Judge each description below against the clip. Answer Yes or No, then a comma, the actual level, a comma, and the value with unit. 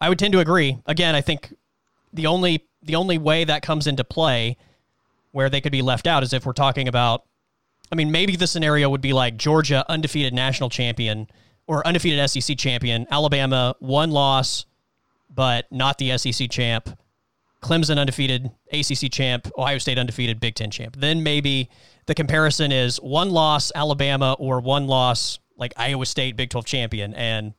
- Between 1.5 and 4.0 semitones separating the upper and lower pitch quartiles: Yes, average, 3.3 semitones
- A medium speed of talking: Yes, average, 175 wpm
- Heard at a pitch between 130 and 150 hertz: Yes, low, 135 Hz